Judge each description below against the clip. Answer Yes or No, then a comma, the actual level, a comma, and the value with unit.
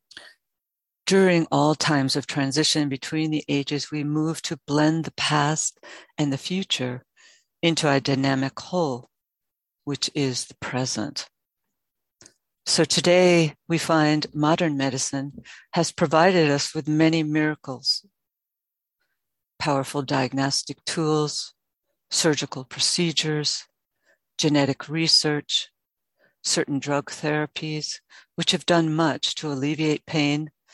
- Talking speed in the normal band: No, slow, 105 wpm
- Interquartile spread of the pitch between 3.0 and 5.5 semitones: No, narrow, 2.5 semitones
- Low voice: No, medium, 150 Hz